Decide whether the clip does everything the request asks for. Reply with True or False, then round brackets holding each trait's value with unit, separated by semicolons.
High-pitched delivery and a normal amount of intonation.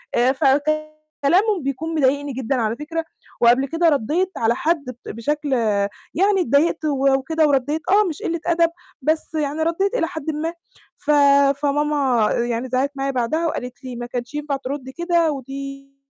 True (290 Hz; 3.5 semitones)